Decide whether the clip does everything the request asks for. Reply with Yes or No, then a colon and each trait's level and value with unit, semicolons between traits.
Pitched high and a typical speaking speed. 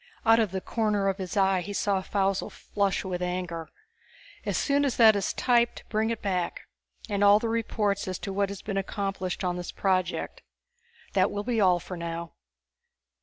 Yes: high, 195 Hz; average, 185 wpm